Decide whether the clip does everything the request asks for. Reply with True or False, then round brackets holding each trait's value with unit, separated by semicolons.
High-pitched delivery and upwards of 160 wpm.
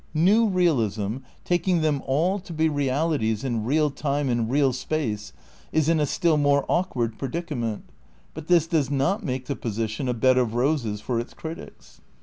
False (140 Hz; 170 wpm)